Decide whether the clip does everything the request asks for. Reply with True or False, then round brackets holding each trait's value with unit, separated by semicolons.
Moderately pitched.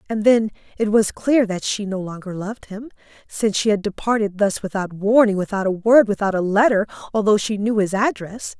False (205 Hz)